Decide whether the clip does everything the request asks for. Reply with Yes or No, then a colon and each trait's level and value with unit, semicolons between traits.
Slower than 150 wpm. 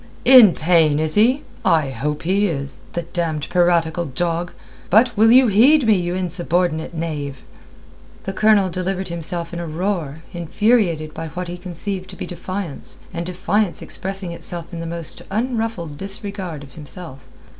No: average, 155 wpm